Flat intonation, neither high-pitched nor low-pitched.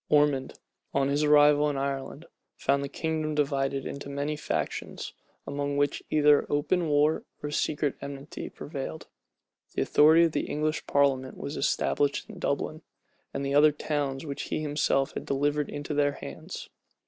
Yes: narrow, 1.2 semitones; medium, 145 Hz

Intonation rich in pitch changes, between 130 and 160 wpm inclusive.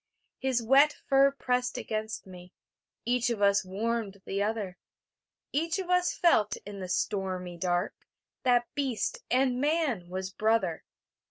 Yes: wide, 5.7 semitones; average, 140 wpm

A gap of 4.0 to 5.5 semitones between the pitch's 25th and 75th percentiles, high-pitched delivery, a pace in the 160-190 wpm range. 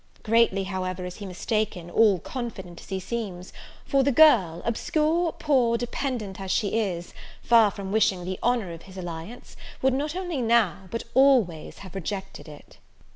Yes: average, 4.7 semitones; high, 210 Hz; average, 165 wpm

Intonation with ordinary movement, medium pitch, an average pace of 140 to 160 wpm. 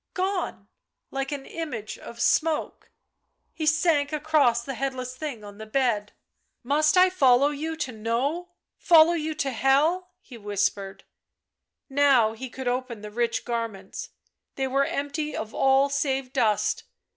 No: average, 4.5 semitones; very high, 270 Hz; average, 155 wpm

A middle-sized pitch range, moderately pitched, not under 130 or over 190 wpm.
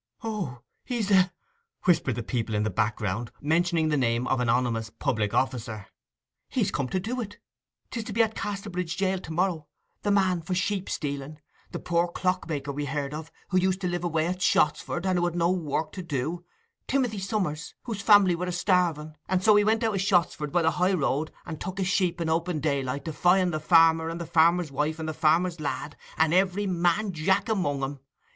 No: average, 4.1 semitones; medium, 170 Hz; average, 200 wpm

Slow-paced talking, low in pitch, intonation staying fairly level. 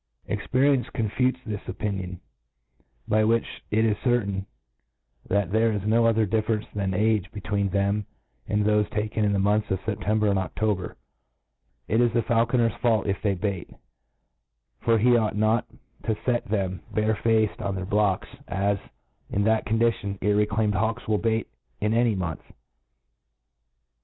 No: average, 155 wpm; low, 105 Hz; narrow, 2.1 semitones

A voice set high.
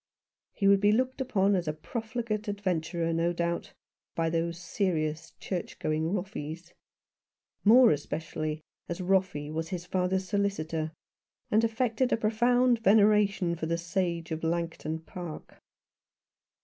No: medium, 180 Hz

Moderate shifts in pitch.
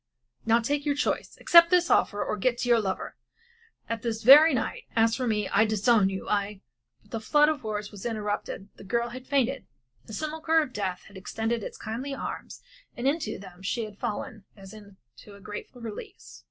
Yes: average, 4.3 semitones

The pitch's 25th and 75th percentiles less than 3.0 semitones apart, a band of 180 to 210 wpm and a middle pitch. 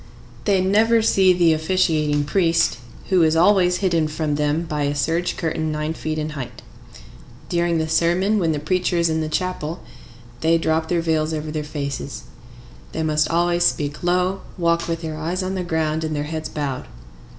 Yes: narrow, 2.4 semitones; average, 185 wpm; medium, 160 Hz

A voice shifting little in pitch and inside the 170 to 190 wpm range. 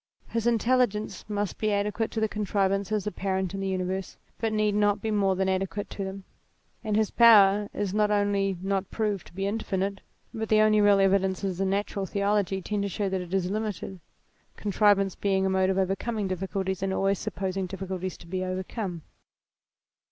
Yes: narrow, 1.6 semitones; average, 180 wpm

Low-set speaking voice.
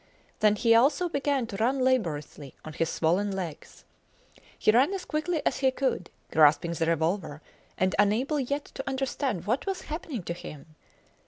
No: high, 225 Hz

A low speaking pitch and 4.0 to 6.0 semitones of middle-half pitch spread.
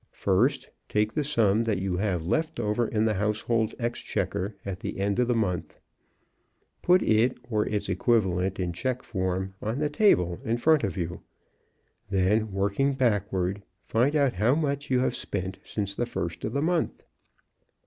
Yes: low, 105 Hz; average, 4.4 semitones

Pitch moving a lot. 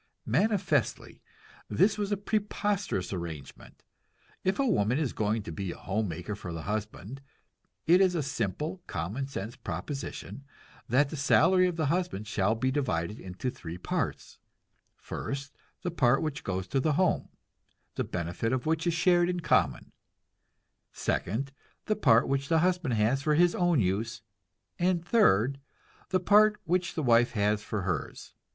Yes: wide, 8.9 semitones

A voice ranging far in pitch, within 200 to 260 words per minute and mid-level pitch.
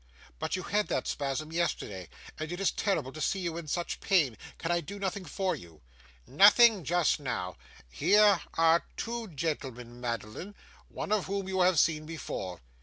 No: wide, 6.3 semitones; average, 175 wpm; medium, 165 Hz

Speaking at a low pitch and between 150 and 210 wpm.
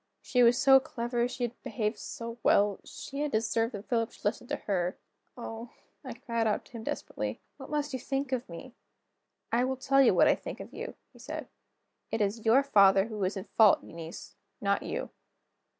No: high, 230 Hz; average, 200 wpm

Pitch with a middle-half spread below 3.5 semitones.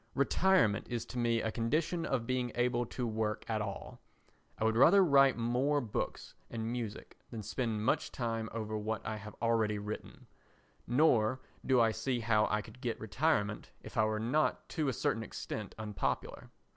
Yes: average, 2.7 semitones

